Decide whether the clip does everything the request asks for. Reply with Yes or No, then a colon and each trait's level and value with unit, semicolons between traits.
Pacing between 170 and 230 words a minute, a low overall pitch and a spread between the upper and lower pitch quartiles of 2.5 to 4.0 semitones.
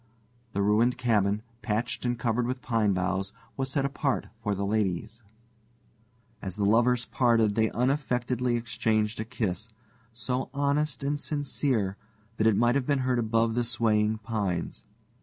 No: average, 150 wpm; low, 115 Hz; average, 2.9 semitones